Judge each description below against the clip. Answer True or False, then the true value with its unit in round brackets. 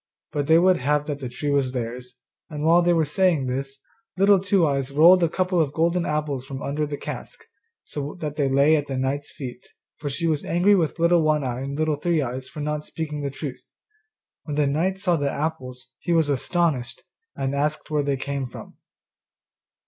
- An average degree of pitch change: True (3.1 semitones)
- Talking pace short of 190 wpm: False (205 wpm)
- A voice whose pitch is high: False (150 Hz)